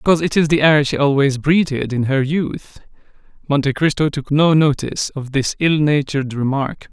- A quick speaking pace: No, average, 180 wpm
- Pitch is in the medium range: Yes, medium, 145 Hz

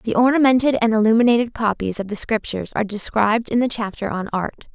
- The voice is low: No, high, 225 Hz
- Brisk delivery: No, average, 190 wpm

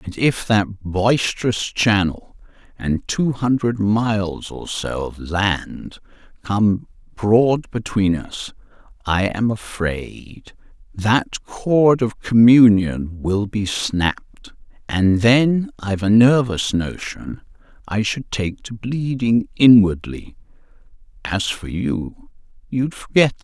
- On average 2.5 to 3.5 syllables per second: Yes, 3.2 syllables/s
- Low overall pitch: Yes, low, 105 Hz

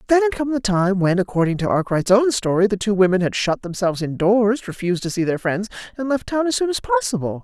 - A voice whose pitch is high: Yes, high, 205 Hz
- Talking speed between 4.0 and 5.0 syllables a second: No, 6.1 syllables/s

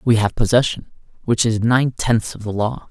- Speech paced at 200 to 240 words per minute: Yes, fast, 205 wpm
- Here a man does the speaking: Yes, male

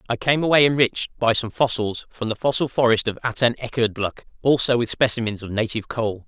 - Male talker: Yes, male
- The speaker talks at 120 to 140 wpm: No, average, 180 wpm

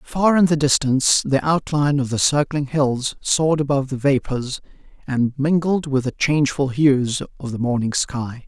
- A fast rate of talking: No, average, 170 wpm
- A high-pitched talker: No, medium, 140 Hz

